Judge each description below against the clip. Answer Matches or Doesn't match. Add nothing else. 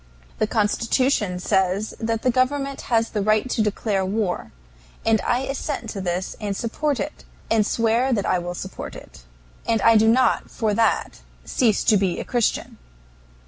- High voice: Matches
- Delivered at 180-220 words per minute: Doesn't match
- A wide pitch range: Doesn't match